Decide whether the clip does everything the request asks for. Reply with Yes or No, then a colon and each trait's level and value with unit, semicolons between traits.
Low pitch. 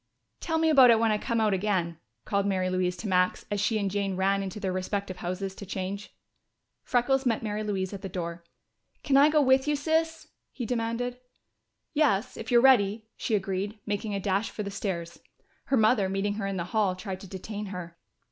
No: high, 205 Hz